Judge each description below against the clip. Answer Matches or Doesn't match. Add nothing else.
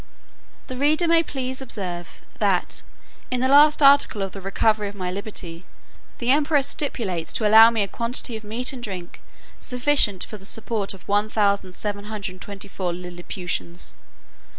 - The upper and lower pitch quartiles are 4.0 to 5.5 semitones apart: Matches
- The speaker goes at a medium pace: Matches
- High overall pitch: Matches